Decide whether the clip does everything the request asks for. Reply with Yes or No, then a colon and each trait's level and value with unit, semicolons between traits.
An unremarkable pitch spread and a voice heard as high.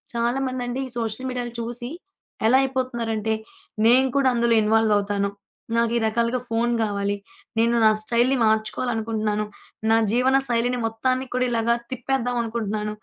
No: narrow, 2.2 semitones; high, 235 Hz